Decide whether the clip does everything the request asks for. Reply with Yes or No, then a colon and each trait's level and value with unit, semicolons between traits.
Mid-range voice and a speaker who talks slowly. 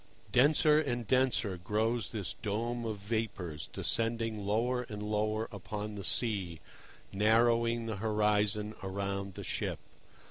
No: low, 110 Hz; slow, 120 wpm